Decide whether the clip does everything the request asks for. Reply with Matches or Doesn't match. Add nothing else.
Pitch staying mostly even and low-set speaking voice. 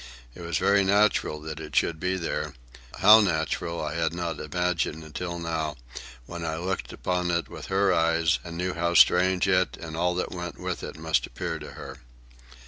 Matches